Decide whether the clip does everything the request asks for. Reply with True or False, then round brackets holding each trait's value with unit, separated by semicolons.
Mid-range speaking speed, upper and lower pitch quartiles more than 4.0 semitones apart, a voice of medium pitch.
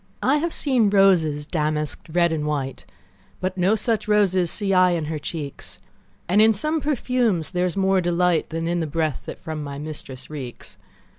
True (180 wpm; 4.8 semitones; 175 Hz)